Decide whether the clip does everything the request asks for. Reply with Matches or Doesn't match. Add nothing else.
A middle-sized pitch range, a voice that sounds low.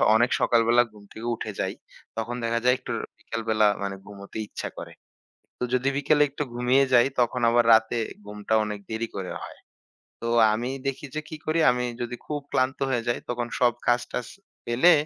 Doesn't match